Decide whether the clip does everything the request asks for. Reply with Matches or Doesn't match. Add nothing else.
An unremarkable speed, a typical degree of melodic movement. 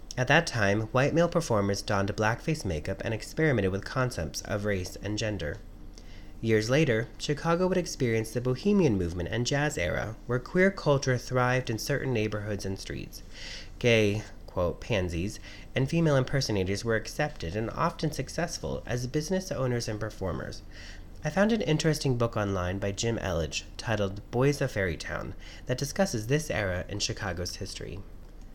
Doesn't match